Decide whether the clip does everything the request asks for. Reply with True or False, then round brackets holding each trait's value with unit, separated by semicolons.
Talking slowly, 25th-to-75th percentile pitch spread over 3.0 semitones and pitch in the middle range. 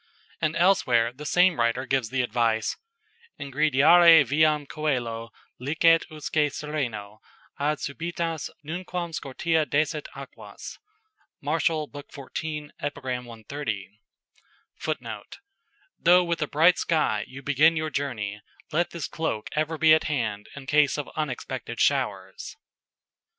True (120 wpm; 3.9 semitones; 150 Hz)